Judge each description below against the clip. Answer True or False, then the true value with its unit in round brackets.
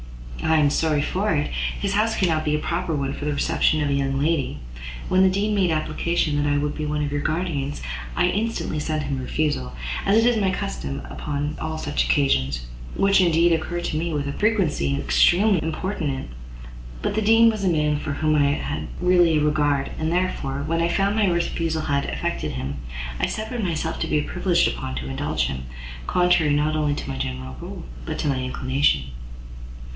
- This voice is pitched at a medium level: True (155 Hz)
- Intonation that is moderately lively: True (3.9 semitones)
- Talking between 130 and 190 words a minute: False (200 wpm)